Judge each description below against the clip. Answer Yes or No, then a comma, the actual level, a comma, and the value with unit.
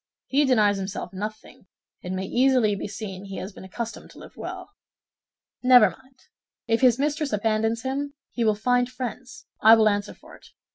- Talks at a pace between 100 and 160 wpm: No, average, 180 wpm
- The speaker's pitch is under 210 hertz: No, high, 225 Hz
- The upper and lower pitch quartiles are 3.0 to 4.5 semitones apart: Yes, average, 3.9 semitones